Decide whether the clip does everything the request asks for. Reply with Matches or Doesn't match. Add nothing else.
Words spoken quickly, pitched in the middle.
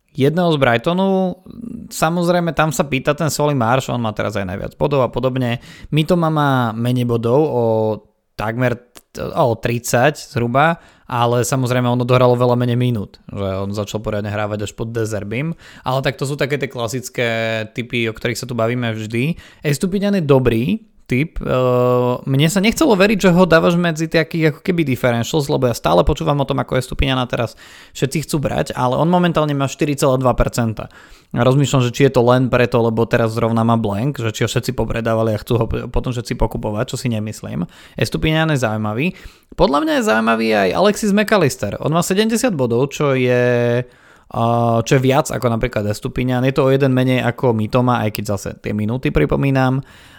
Doesn't match